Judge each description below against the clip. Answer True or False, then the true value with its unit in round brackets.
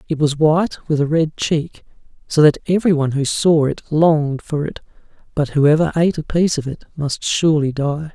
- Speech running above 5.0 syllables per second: True (5.5 syllables/s)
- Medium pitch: True (155 Hz)